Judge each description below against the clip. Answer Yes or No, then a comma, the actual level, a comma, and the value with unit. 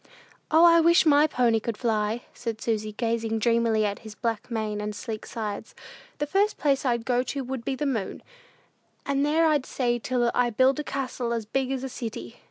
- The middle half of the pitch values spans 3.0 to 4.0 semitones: Yes, average, 3.6 semitones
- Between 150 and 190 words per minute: No, average, 200 wpm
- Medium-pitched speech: No, high, 240 Hz